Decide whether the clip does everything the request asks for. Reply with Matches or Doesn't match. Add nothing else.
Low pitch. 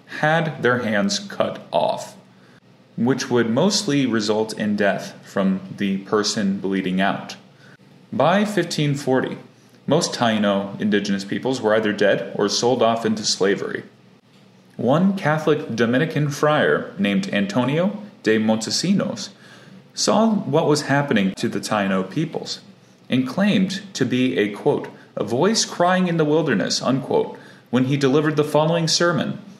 Matches